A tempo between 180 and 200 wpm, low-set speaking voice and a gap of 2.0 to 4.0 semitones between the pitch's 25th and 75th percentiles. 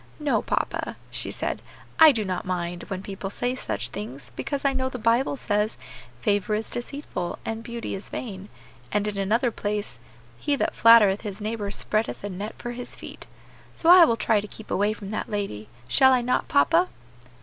No: average, 190 wpm; high, 215 Hz; average, 3.5 semitones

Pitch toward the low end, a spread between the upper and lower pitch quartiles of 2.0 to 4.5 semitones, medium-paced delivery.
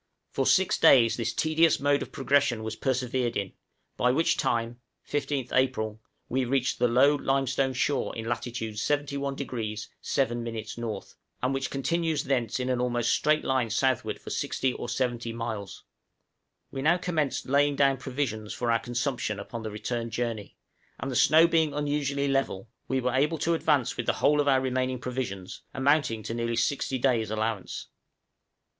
Yes: low, 130 Hz; average, 3.2 semitones; average, 165 wpm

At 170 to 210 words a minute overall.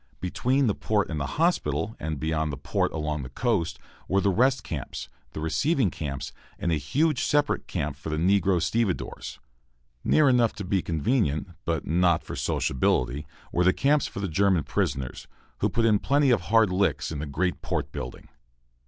Yes: average, 180 wpm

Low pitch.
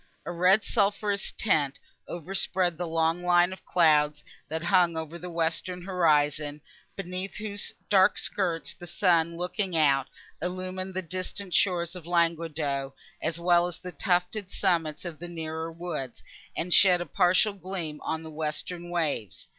No: medium, 175 Hz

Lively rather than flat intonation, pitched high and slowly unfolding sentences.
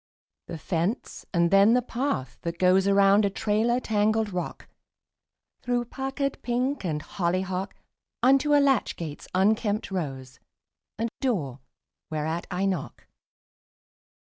Yes: wide, 5.7 semitones; high, 200 Hz; slow, 120 wpm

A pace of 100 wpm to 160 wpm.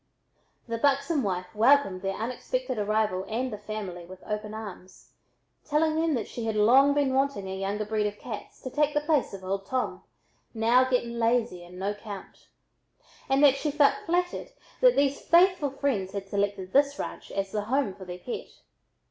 No: average, 180 wpm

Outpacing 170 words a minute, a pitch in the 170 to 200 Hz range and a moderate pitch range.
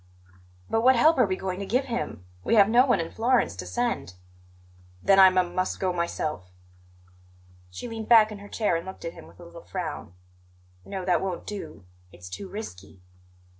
Yes: average, 195 wpm; high, 190 Hz; average, 4.9 semitones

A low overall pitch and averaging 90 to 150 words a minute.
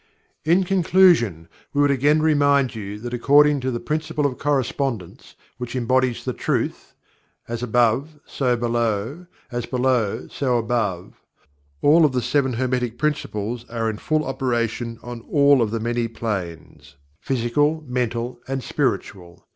Yes: low, 125 Hz; average, 140 wpm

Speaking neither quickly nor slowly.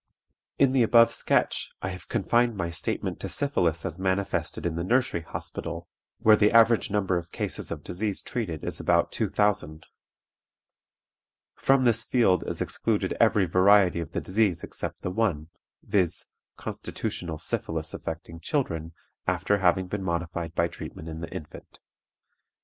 Yes: average, 150 wpm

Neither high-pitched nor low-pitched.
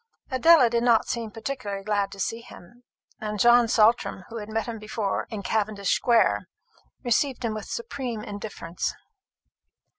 No: high, 225 Hz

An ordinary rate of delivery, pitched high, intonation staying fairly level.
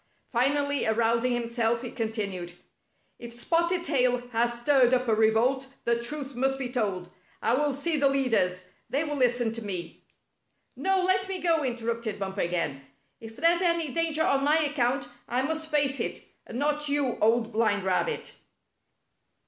No: average, 165 wpm; very high, 250 Hz; average, 4.3 semitones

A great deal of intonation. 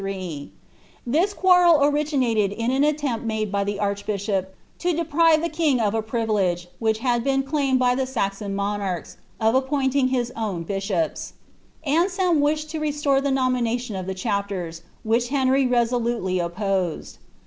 Yes: wide, 5.9 semitones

